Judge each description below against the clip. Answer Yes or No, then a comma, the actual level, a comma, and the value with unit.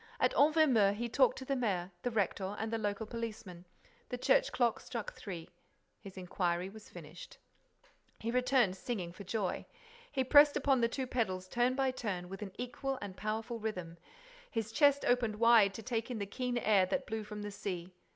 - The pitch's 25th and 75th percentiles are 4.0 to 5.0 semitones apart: Yes, average, 4.3 semitones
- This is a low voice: No, high, 220 Hz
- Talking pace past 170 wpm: Yes, average, 190 wpm